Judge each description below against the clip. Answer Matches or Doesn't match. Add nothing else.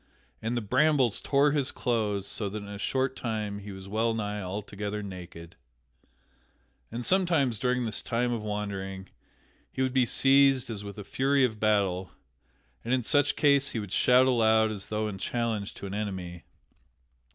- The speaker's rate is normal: Matches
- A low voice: Matches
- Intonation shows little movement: Doesn't match